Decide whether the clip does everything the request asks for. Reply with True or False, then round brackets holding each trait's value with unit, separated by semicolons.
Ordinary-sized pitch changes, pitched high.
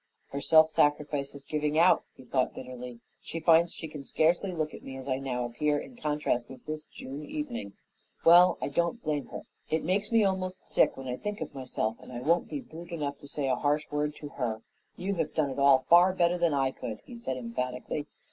False (4.4 semitones; 150 Hz)